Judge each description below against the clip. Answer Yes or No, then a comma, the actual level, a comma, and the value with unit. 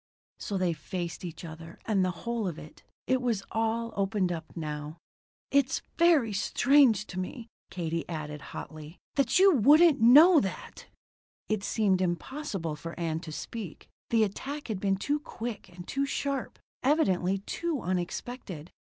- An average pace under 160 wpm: Yes, average, 150 wpm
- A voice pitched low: No, high, 200 Hz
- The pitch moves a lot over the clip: Yes, wide, 7.0 semitones